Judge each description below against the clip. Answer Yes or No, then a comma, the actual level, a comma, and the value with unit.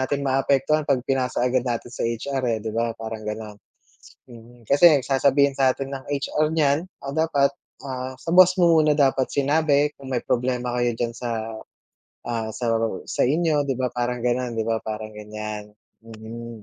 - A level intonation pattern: No, average, 3.4 semitones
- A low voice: Yes, low, 125 Hz